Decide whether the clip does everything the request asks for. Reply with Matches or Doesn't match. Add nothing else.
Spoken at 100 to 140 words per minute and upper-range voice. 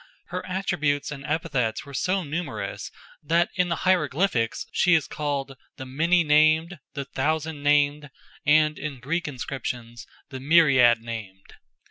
Doesn't match